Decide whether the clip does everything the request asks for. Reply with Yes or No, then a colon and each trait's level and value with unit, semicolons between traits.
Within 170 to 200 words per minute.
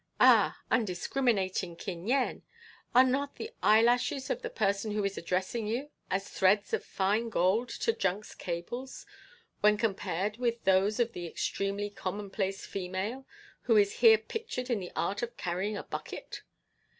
No: average, 150 wpm